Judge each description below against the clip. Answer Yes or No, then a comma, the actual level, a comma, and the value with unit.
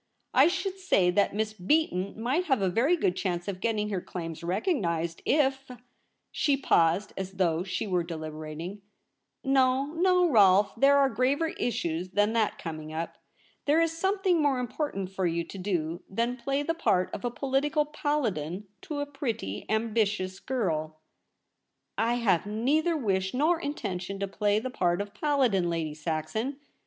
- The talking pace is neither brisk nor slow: Yes, average, 165 wpm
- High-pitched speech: Yes, high, 215 Hz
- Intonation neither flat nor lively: No, wide, 7.7 semitones